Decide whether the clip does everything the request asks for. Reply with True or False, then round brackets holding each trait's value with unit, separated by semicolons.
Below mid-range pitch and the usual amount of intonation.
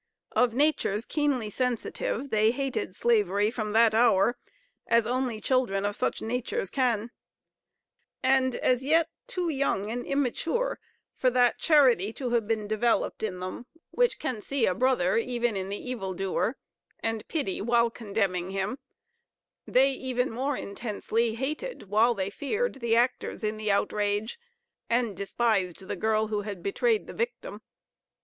False (235 Hz; 3.8 semitones)